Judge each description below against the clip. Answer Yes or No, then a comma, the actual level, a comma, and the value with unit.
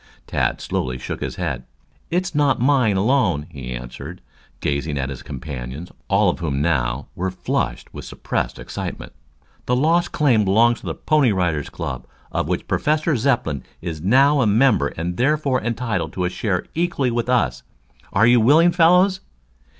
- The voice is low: Yes, low, 105 Hz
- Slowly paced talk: No, average, 165 wpm